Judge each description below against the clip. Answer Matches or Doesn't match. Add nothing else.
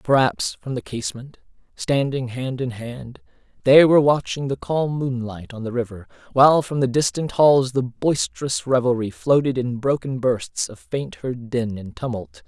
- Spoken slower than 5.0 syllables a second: Matches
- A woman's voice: Doesn't match